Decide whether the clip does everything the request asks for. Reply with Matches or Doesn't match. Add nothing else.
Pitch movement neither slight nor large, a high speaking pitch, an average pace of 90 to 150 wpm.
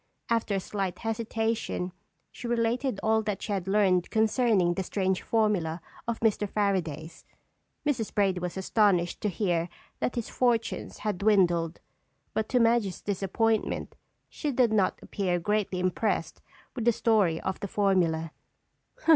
Matches